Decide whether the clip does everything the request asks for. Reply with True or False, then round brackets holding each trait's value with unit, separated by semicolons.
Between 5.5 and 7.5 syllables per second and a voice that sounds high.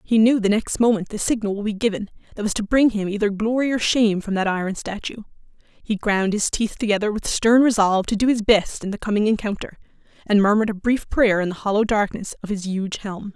True (5.9 syllables/s; 210 Hz)